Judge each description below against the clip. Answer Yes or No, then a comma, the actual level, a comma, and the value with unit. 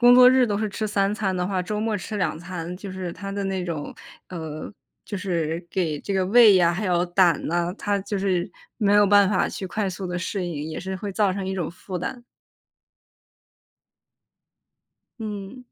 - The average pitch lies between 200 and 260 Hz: No, high, 190 Hz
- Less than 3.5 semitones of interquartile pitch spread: Yes, average, 2.7 semitones